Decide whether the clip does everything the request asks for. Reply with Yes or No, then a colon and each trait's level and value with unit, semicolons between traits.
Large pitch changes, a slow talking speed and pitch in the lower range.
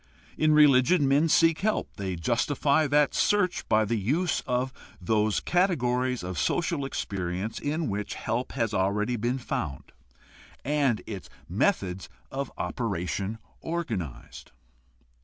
Yes: wide, 6.6 semitones; slow, 125 wpm; low, 125 Hz